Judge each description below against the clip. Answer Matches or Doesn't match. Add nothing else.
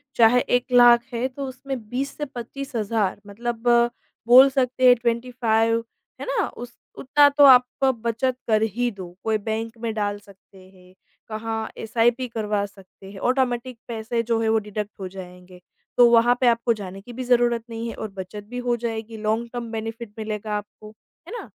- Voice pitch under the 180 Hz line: Doesn't match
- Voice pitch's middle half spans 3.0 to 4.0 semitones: Doesn't match